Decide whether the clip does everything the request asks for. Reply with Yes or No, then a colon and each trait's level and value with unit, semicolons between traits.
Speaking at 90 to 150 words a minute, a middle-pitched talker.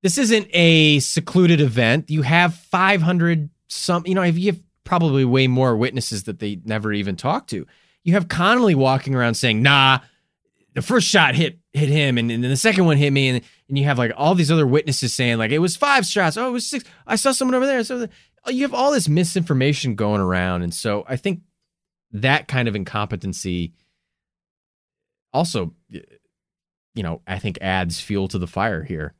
No: average, 195 wpm; medium, 145 Hz